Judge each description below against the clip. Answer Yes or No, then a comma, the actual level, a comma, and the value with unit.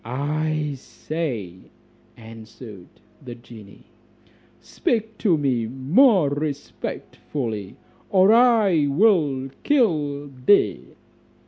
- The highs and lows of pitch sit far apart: Yes, wide, 7.0 semitones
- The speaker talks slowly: Yes, slow, 80 wpm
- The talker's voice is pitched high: No, medium, 145 Hz